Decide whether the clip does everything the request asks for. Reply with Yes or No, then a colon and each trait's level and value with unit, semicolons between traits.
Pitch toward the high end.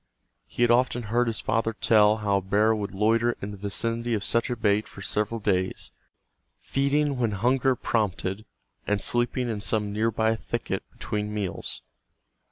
No: low, 110 Hz